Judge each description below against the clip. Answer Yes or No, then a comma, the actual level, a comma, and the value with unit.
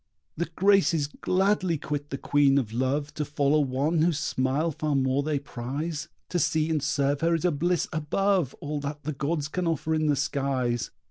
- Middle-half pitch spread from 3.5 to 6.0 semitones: No, average, 2.7 semitones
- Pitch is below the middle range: No, medium, 150 Hz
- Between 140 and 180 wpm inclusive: No, average, 190 wpm